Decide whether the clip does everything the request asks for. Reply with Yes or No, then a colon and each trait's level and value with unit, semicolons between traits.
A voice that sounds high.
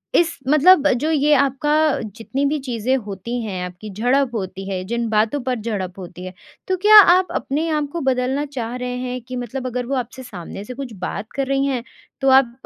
Yes: very high, 255 Hz